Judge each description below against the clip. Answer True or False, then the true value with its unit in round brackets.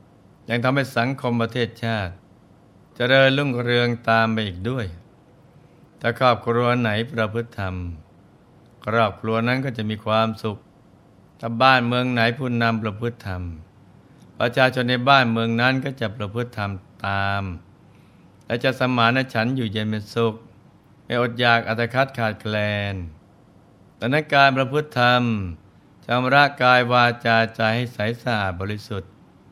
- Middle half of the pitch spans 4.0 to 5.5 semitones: False (3.1 semitones)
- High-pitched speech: False (115 Hz)